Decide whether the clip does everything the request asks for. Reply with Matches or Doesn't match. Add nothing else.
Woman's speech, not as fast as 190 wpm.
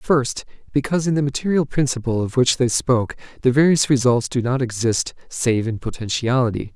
Doesn't match